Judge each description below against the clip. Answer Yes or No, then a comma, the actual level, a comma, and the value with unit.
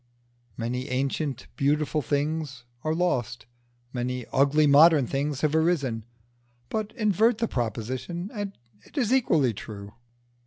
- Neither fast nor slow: No, slow, 120 wpm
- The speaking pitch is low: No, medium, 145 Hz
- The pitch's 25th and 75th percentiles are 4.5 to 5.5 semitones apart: Yes, average, 5.2 semitones